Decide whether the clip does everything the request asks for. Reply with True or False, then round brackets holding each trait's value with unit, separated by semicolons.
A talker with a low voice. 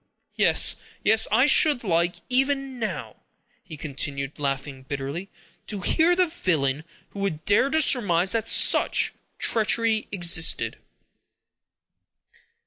False (195 Hz)